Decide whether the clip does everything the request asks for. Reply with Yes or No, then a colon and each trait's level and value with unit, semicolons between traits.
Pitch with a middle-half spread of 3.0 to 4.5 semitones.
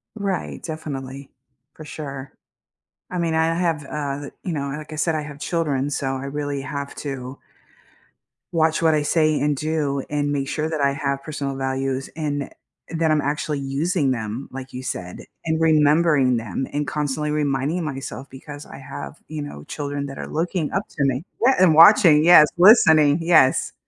No: narrow, 2.5 semitones